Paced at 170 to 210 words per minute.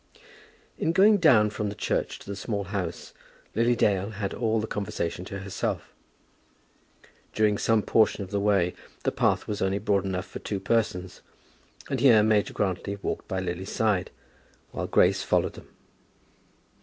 No: average, 160 wpm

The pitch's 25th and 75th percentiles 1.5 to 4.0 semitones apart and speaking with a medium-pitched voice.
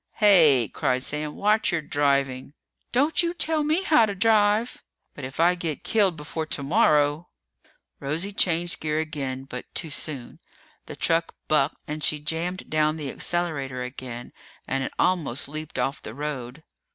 No: average, 4.7 semitones; medium, 155 Hz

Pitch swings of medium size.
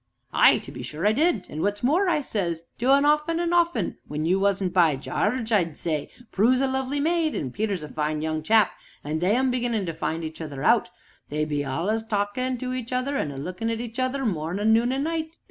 No: wide, 8.1 semitones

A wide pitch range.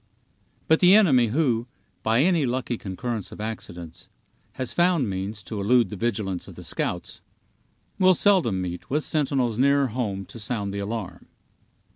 Yes: wide, 5.8 semitones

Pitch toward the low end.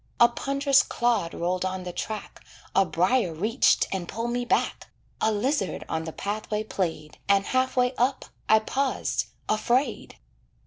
No: high, 215 Hz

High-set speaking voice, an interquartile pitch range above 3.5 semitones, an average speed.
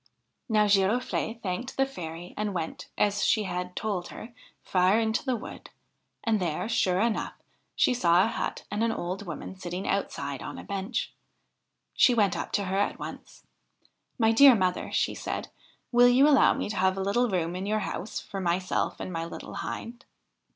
Yes: high, 200 Hz; average, 3.9 semitones; average, 190 wpm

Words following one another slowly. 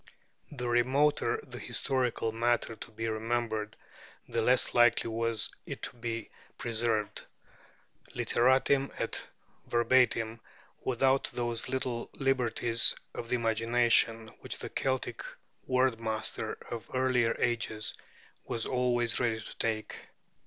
Yes: slow, 115 wpm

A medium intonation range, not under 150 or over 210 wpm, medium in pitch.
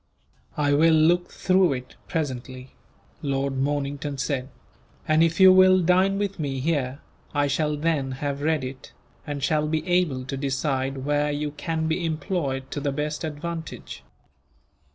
Yes: average, 3.1 semitones; average, 155 wpm; medium, 150 Hz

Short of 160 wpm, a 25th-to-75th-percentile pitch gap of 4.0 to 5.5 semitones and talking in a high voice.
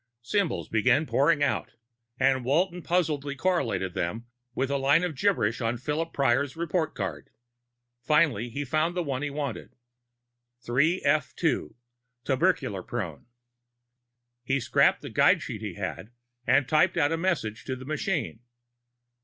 No: slow, 135 wpm; average, 5.0 semitones; medium, 140 Hz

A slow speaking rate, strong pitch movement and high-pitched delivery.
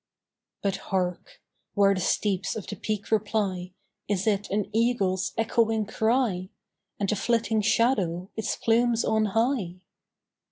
No: slow, 130 wpm; average, 2.9 semitones; high, 210 Hz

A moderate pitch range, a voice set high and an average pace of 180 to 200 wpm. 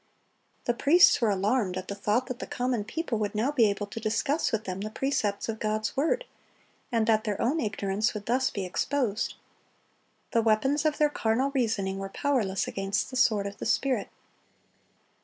Yes: average, 4.3 semitones; high, 225 Hz; average, 185 wpm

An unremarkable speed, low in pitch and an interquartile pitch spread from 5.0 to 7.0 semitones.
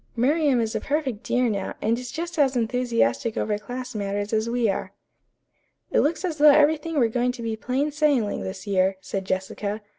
No: average, 190 wpm; high, 240 Hz; average, 5.3 semitones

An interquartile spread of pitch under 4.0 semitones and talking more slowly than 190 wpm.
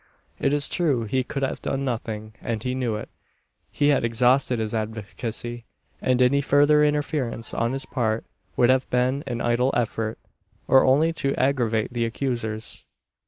Yes: average, 3.1 semitones; average, 165 wpm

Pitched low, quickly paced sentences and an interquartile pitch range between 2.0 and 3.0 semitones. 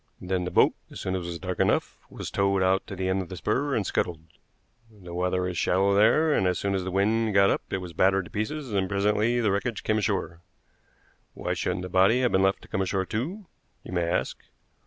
Yes: very low, 95 Hz; fast, 240 wpm; narrow, 2.6 semitones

